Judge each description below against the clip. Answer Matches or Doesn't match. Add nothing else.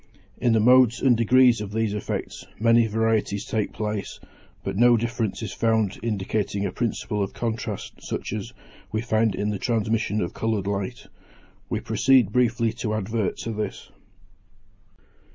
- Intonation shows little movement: Matches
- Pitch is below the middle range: Matches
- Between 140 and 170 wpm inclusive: Matches